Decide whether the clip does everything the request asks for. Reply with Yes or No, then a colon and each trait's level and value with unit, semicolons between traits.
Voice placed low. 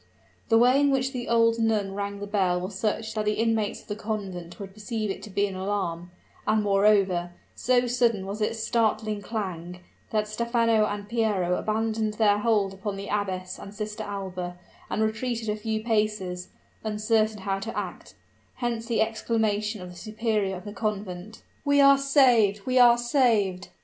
No: high, 215 Hz